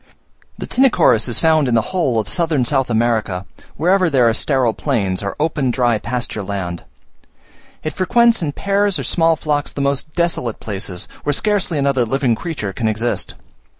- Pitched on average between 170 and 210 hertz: No, low, 135 Hz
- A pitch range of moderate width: No, wide, 6.3 semitones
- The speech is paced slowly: No, average, 170 wpm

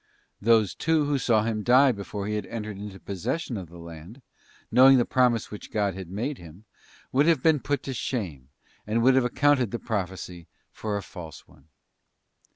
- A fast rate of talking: No, average, 185 wpm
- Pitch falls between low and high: No, low, 110 Hz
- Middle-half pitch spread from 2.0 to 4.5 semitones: No, average, 5.2 semitones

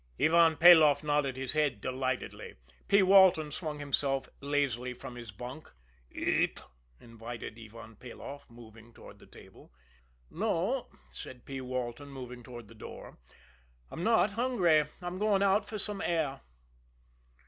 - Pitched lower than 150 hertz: Yes, medium, 140 Hz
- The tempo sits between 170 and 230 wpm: No, slow, 135 wpm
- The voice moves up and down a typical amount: No, wide, 5.7 semitones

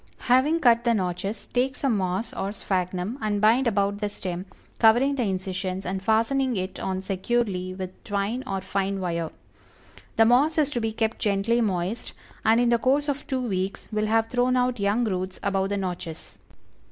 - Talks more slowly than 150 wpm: No, average, 180 wpm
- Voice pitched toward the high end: Yes, high, 210 Hz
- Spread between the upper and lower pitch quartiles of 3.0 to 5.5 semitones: Yes, average, 4.2 semitones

